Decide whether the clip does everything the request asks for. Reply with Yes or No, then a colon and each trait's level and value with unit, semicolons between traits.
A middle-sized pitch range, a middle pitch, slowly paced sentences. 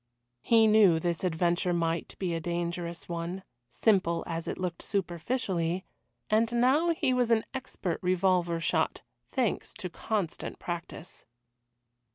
Yes: average, 4.3 semitones; medium, 180 Hz; slow, 130 wpm